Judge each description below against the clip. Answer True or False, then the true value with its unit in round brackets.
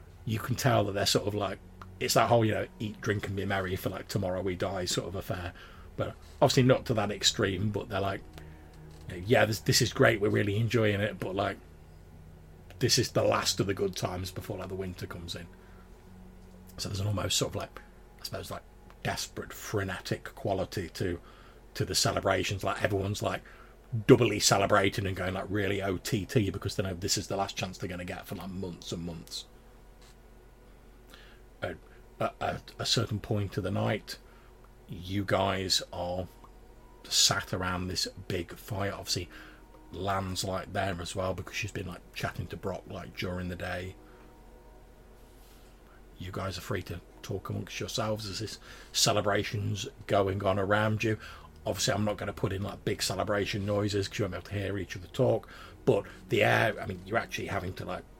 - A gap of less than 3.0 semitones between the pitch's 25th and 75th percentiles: True (2.6 semitones)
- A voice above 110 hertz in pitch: False (100 Hz)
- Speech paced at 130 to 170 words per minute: False (185 wpm)